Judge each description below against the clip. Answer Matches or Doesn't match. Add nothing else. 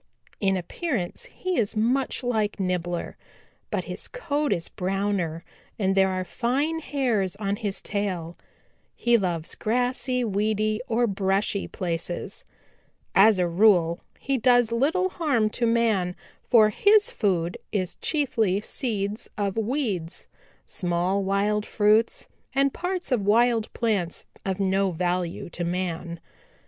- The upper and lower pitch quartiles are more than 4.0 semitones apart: Matches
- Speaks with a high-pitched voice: Matches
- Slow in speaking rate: Matches